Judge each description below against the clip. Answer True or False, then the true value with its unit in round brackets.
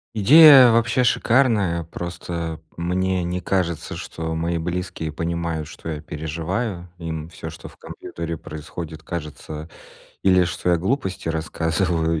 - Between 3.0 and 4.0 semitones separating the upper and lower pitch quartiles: False (2.5 semitones)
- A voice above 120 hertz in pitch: False (85 Hz)